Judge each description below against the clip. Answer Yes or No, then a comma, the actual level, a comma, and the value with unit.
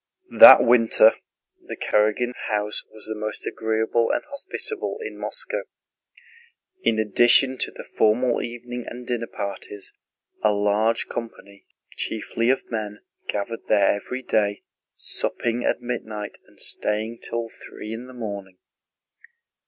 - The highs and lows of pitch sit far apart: No, narrow, 2.4 semitones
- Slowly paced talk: Yes, slow, 130 wpm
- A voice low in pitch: Yes, low, 110 Hz